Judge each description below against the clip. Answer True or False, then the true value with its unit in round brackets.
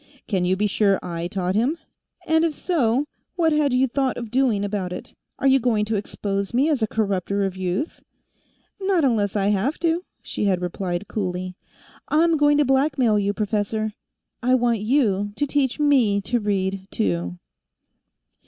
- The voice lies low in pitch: False (215 Hz)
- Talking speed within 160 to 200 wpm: True (170 wpm)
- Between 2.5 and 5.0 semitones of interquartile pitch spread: False (5.6 semitones)